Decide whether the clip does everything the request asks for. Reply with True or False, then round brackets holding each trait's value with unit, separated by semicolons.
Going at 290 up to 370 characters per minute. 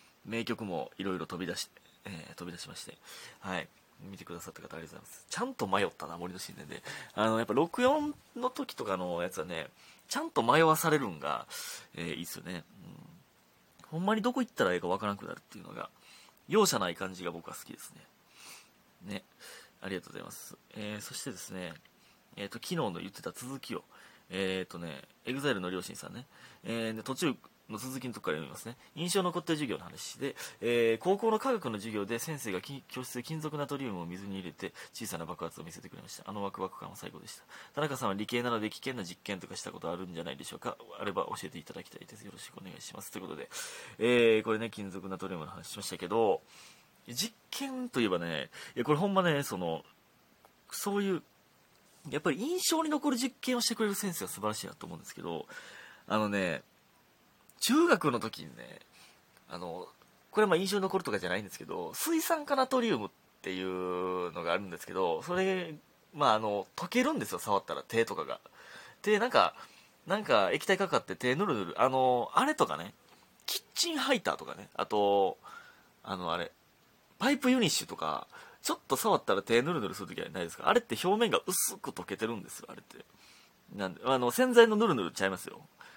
False (410 characters per minute)